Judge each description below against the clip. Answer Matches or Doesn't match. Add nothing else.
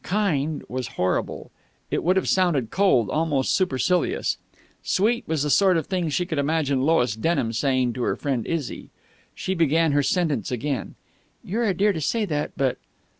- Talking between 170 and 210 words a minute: Matches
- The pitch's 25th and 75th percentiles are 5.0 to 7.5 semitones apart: Matches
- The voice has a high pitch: Doesn't match